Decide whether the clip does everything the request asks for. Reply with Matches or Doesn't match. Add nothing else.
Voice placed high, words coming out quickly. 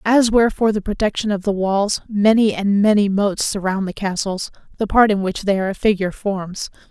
Matches